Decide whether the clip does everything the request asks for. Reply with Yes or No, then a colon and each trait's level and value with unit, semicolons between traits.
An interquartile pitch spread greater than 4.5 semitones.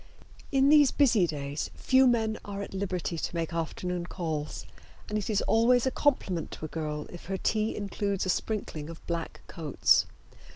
Yes: average, 5.1 semitones